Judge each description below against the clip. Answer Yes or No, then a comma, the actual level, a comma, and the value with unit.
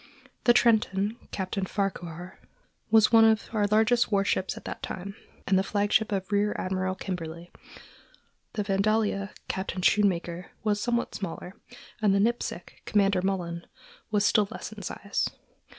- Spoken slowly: No, average, 145 wpm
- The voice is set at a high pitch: Yes, high, 200 Hz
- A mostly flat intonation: Yes, narrow, 2.3 semitones